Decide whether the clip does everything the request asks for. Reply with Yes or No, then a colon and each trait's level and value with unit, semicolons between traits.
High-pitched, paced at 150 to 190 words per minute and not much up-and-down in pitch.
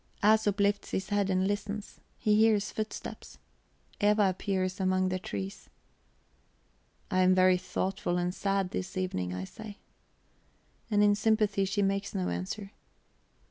No: high, 195 Hz; average, 140 wpm; narrow, 1.9 semitones